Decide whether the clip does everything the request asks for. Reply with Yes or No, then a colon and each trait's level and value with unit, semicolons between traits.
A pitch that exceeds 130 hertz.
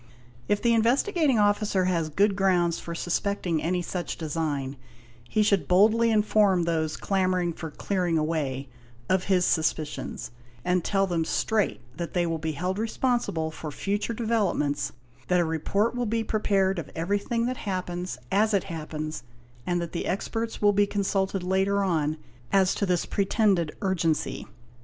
Yes: medium, 185 Hz